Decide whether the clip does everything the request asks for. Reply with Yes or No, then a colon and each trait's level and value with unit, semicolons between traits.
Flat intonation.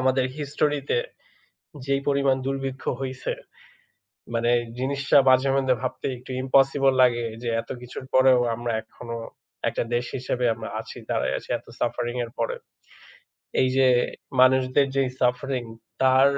Yes: narrow, 1.6 semitones